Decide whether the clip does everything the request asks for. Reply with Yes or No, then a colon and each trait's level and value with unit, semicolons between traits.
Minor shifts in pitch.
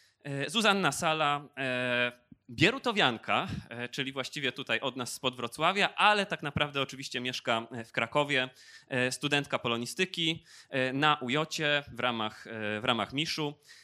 No: average, 3.4 semitones